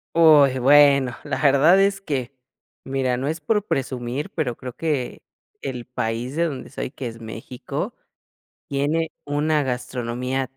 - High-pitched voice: No, low, 135 Hz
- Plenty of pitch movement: No, average, 3.3 semitones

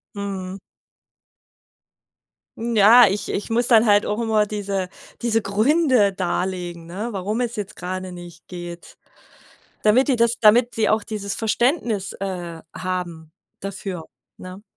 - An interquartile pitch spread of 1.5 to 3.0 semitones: No, average, 3.5 semitones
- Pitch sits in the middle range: No, high, 200 Hz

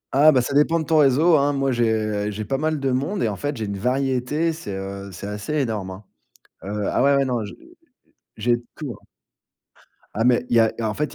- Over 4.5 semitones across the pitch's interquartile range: Yes, average, 5.2 semitones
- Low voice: Yes, low, 125 Hz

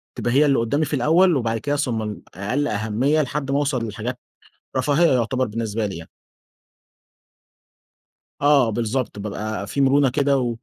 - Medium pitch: No, low, 125 Hz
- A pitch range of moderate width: Yes, average, 4.3 semitones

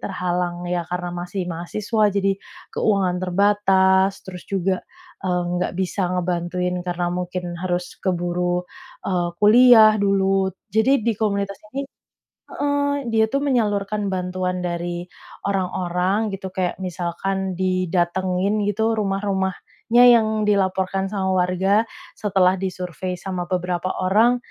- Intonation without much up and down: Yes, narrow, 2.0 semitones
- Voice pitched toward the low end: No, high, 190 Hz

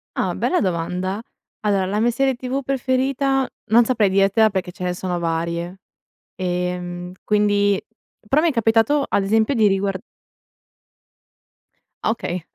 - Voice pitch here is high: Yes, high, 205 Hz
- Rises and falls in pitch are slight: No, average, 4.9 semitones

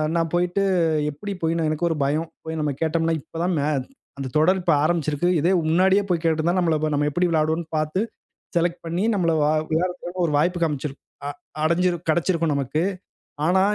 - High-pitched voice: No, medium, 165 Hz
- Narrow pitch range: Yes, narrow, 2.2 semitones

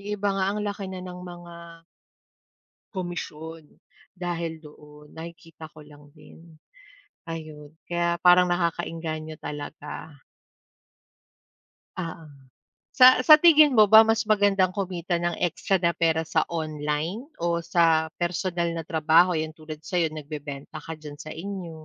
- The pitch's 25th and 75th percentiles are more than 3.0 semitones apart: No, narrow, 2.4 semitones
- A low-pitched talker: No, medium, 165 Hz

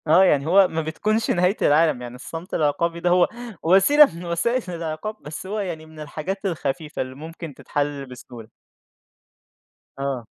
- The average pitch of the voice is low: No, medium, 165 Hz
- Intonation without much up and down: No, average, 3.8 semitones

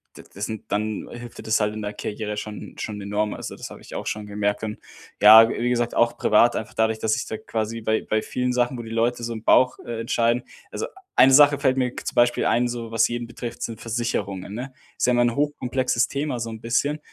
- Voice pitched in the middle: No, low, 115 Hz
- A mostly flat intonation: Yes, narrow, 2.1 semitones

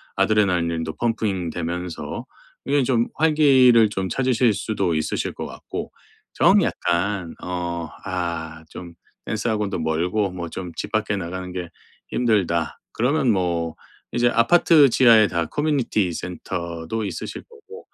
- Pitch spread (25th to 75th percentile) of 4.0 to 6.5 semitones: Yes, wide, 5.4 semitones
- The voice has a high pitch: No, very low, 95 Hz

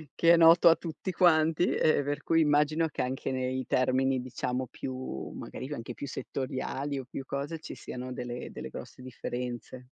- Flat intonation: No, average, 3.5 semitones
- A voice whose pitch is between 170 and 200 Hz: No, low, 135 Hz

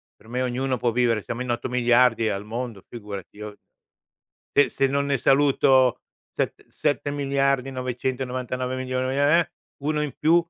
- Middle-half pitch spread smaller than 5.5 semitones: Yes, narrow, 2.4 semitones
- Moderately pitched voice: No, low, 125 Hz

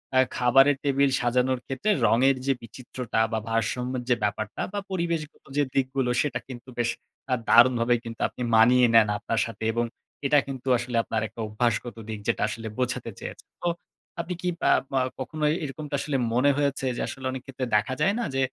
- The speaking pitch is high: No, low, 125 Hz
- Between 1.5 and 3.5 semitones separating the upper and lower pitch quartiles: Yes, average, 2.7 semitones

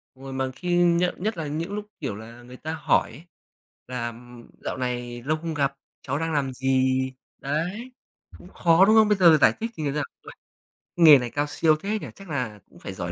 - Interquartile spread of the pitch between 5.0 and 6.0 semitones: Yes, average, 5.3 semitones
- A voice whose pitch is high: No, medium, 145 Hz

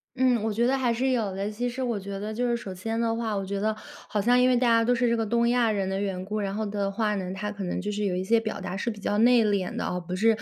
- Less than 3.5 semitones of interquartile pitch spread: Yes, average, 3.1 semitones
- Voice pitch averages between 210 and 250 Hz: Yes, high, 215 Hz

